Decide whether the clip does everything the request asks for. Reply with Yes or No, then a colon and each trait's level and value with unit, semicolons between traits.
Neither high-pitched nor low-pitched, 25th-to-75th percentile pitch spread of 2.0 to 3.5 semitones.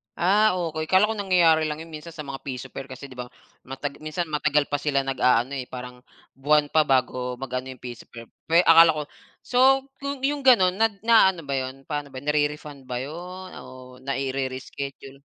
No: medium, 145 Hz; average, 4.7 semitones